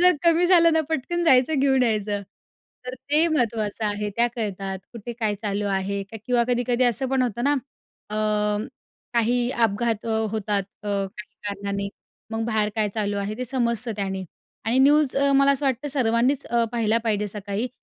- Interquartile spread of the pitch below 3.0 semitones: No, average, 3.8 semitones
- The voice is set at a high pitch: Yes, high, 230 Hz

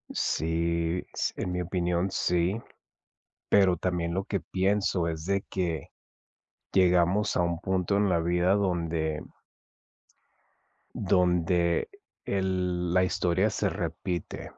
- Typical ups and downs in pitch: No, narrow, 1.9 semitones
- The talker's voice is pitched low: Yes, very low, 90 Hz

